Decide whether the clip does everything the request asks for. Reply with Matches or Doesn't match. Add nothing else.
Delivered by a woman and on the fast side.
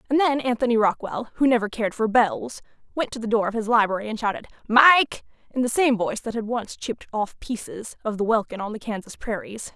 Matches